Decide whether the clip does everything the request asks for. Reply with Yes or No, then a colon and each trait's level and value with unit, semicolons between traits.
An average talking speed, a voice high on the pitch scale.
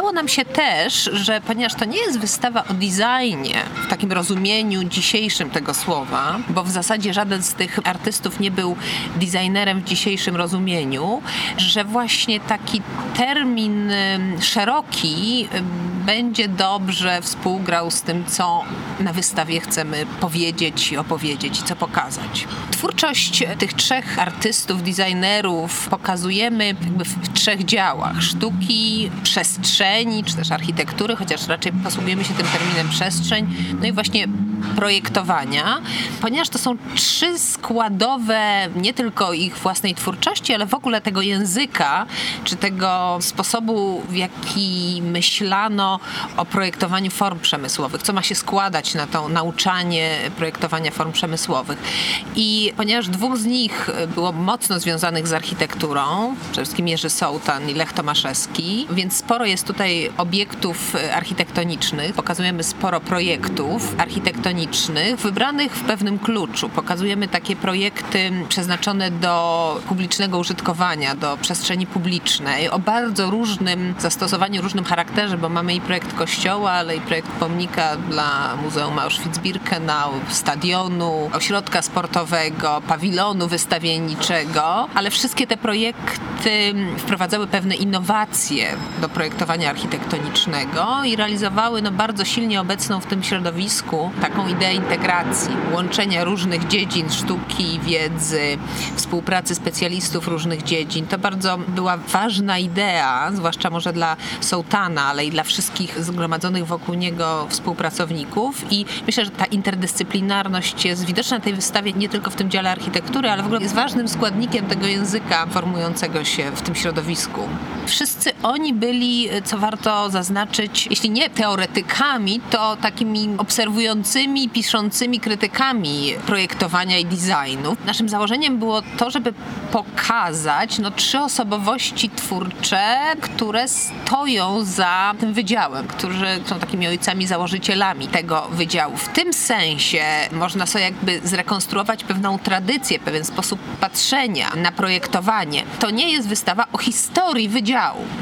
Yes: average, 125 wpm; high, 195 Hz